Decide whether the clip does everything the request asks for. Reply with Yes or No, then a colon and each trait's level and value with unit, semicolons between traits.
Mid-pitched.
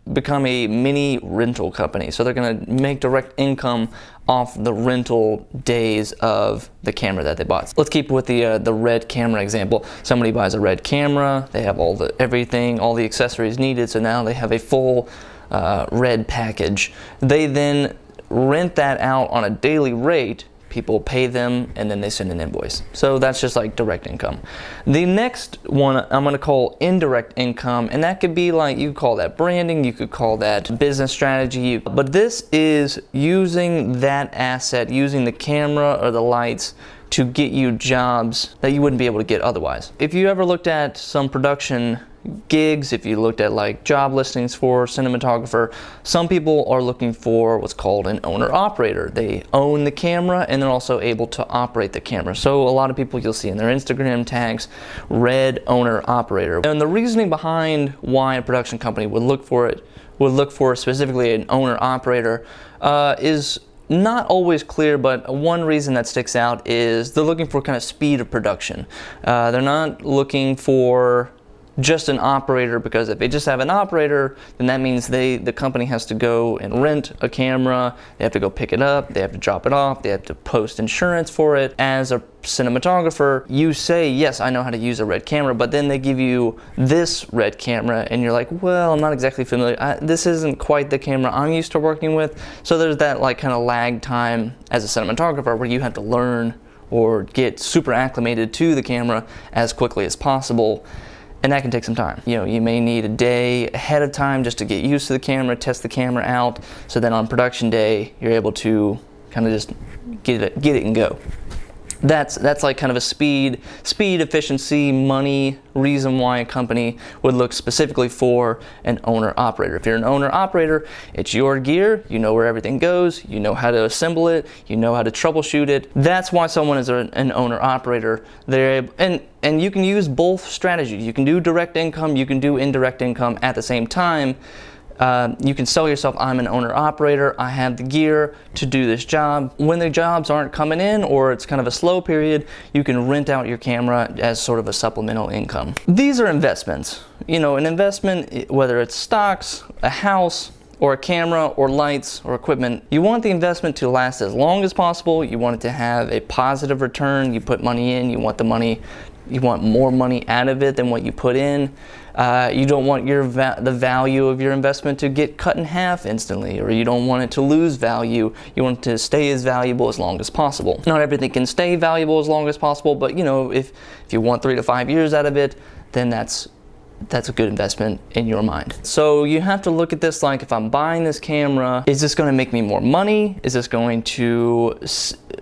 No: low, 130 Hz